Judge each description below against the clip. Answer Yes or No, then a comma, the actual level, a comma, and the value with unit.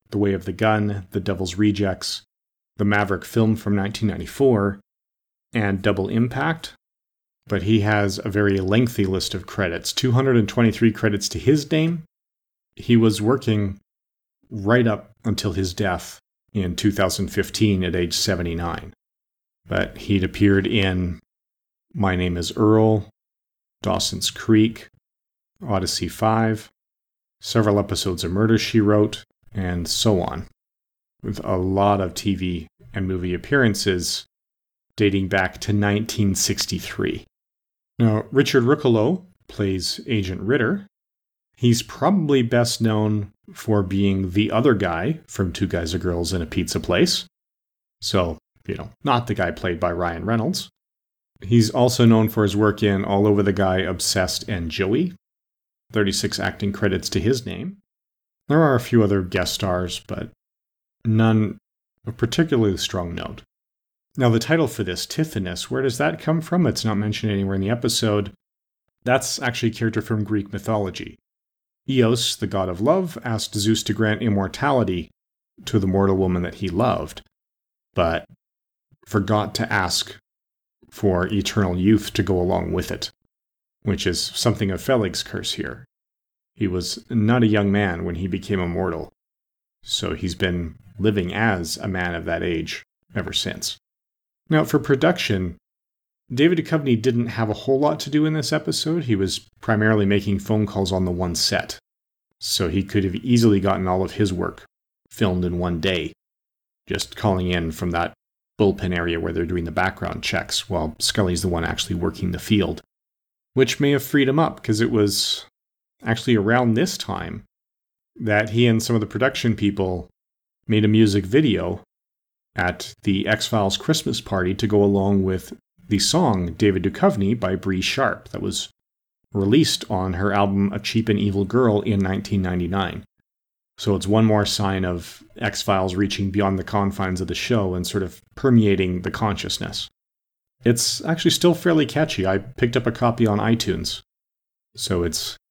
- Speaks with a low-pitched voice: Yes, low, 105 Hz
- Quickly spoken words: No, average, 155 wpm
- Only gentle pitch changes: No, average, 3.2 semitones